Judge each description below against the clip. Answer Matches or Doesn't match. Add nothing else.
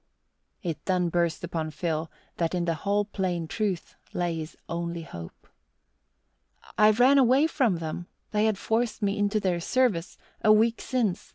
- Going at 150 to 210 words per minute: Matches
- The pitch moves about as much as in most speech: Matches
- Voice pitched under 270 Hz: Matches